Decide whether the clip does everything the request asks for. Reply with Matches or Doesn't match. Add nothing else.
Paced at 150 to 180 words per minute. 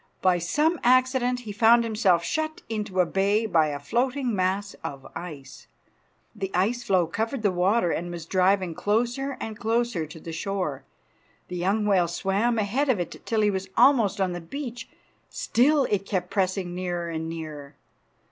Matches